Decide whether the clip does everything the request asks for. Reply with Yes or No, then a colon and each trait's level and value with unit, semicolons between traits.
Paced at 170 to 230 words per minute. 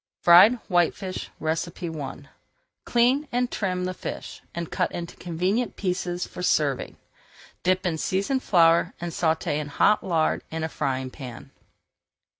No: slow, 135 wpm